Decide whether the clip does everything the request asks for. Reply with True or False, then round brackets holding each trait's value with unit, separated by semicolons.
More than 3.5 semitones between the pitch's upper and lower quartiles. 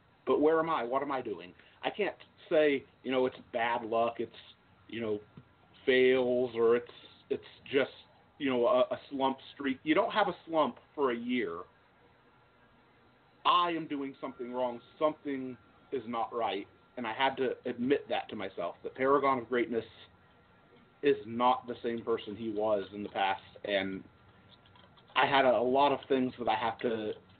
False (3.2 semitones)